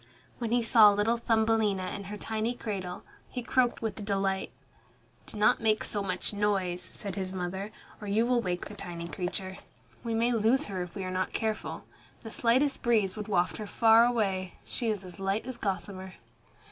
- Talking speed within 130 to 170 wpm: No, average, 185 wpm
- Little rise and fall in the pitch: No, average, 3.2 semitones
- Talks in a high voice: Yes, high, 210 Hz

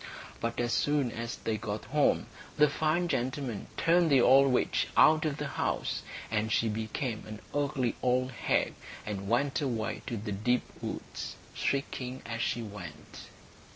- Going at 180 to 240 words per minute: No, average, 155 wpm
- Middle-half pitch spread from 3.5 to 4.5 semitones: Yes, average, 4.2 semitones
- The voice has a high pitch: No, low, 125 Hz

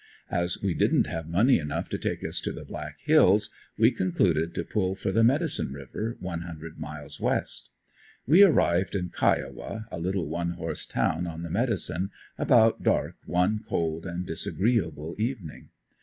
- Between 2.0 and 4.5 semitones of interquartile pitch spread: No, average, 4.9 semitones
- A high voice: No, very low, 90 Hz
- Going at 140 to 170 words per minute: Yes, average, 165 wpm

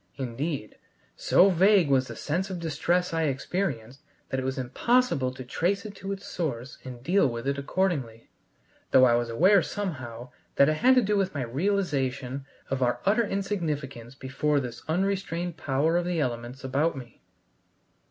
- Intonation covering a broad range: Yes, wide, 6.2 semitones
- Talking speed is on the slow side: No, average, 170 wpm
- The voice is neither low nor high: Yes, medium, 145 Hz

